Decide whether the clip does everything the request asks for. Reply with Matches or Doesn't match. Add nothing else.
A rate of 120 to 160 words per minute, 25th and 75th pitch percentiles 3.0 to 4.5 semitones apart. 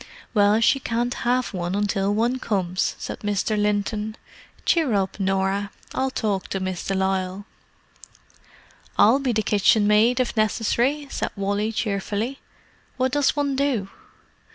Matches